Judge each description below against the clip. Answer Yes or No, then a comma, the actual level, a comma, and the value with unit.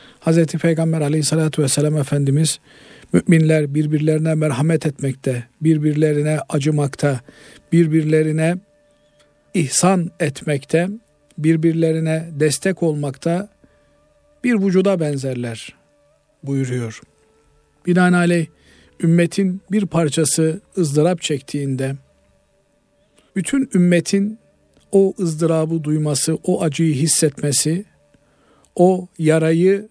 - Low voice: No, medium, 160 Hz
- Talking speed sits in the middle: No, slow, 75 wpm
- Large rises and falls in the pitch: No, average, 2.7 semitones